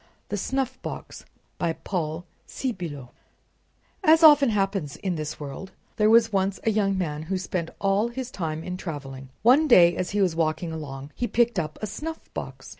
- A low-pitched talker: No, high, 190 Hz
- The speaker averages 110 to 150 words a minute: No, average, 170 wpm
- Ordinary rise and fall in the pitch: No, wide, 6.0 semitones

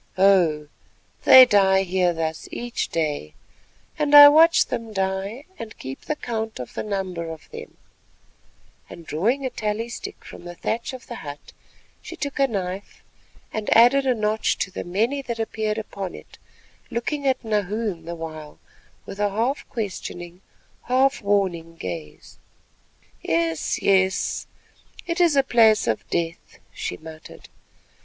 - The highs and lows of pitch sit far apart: Yes, wide, 5.8 semitones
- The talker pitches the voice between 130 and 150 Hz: No, high, 205 Hz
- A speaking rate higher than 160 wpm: No, average, 150 wpm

